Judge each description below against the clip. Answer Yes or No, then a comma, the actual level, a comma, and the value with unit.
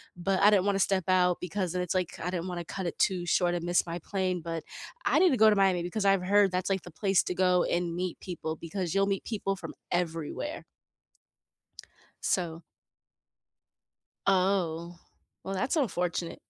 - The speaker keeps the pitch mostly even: Yes, narrow, 2.1 semitones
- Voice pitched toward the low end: No, medium, 180 Hz